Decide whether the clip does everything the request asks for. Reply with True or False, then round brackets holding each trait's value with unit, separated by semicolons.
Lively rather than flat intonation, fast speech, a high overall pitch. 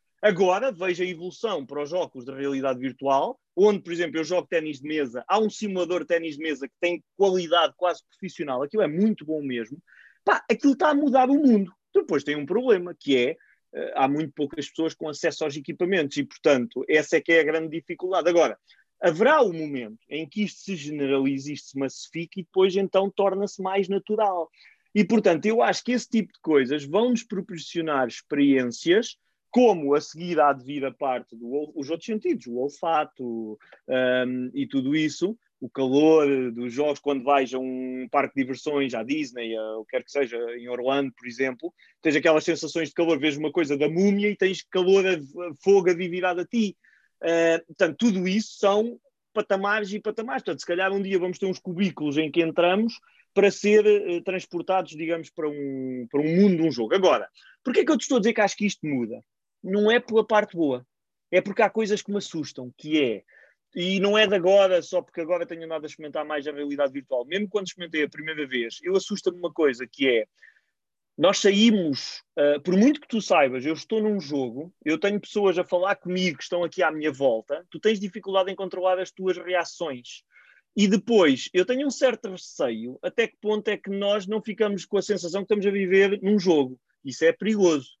False (5.7 semitones; 200 wpm; 175 Hz)